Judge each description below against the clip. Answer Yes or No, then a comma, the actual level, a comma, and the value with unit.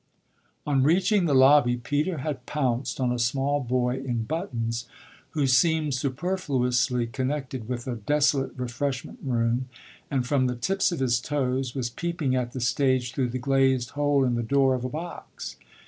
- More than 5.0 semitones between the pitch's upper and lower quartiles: No, average, 2.8 semitones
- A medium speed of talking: Yes, average, 165 wpm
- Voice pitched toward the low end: Yes, low, 130 Hz